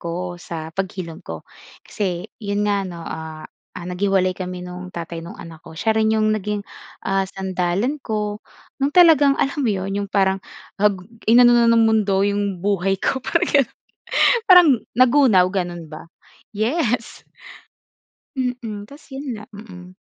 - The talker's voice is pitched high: Yes, high, 200 Hz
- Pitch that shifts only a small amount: No, average, 4.0 semitones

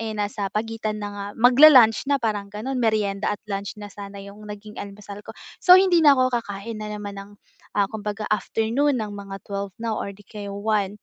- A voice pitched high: Yes, high, 210 Hz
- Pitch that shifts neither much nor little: No, narrow, 1.9 semitones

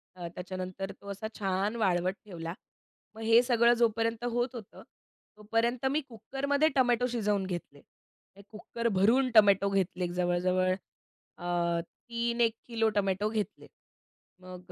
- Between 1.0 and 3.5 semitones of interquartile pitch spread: No, average, 4.2 semitones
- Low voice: No, high, 210 Hz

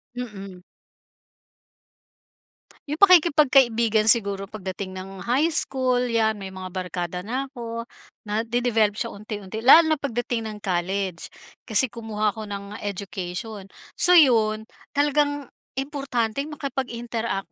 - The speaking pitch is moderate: No, high, 225 Hz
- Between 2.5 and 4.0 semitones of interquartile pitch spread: No, average, 4.6 semitones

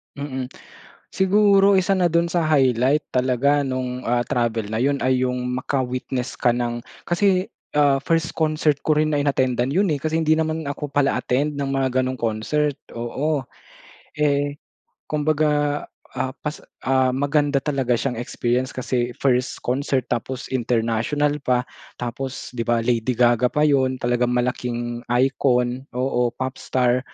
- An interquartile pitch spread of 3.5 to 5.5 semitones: No, average, 3.1 semitones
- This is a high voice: No, low, 130 Hz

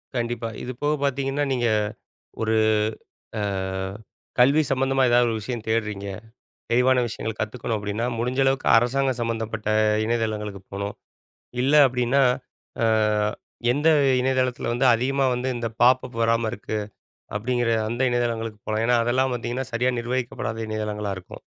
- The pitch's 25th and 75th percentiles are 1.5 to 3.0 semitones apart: Yes, narrow, 2.4 semitones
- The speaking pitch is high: No, low, 120 Hz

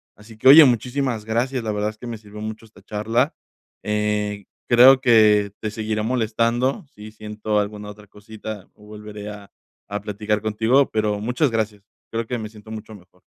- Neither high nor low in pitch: No, low, 110 Hz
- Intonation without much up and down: Yes, narrow, 1.7 semitones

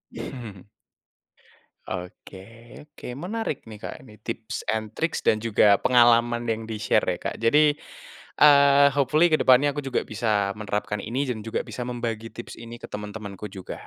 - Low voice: Yes, low, 115 Hz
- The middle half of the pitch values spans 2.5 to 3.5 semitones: No, average, 3.9 semitones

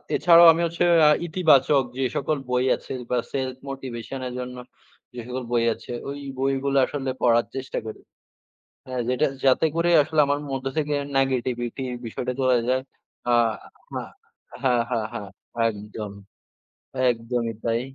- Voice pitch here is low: Yes, low, 130 Hz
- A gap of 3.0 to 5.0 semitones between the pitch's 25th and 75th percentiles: No, narrow, 2.4 semitones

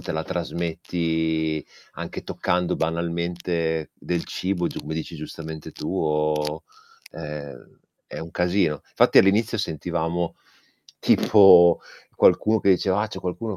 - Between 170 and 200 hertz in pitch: No, very low, 85 Hz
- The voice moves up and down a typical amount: No, narrow, 2.2 semitones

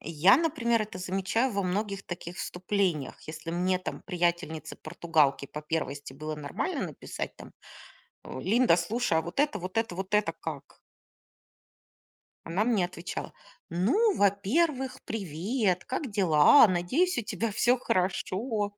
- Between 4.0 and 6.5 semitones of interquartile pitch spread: Yes, average, 5.0 semitones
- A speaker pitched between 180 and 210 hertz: Yes, medium, 185 Hz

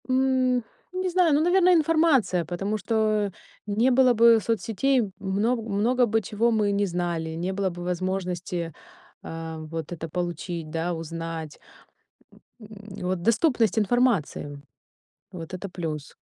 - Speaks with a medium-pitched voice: No, high, 200 Hz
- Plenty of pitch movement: Yes, wide, 6.0 semitones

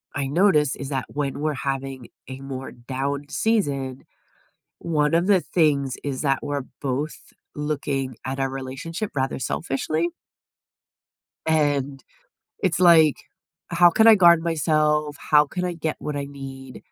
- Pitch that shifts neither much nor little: Yes, average, 3.0 semitones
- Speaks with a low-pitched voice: No, medium, 145 Hz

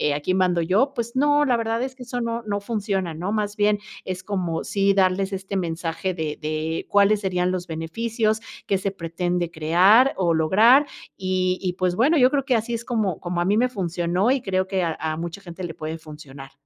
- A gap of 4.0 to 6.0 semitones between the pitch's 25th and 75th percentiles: Yes, average, 4.5 semitones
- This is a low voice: No, high, 190 Hz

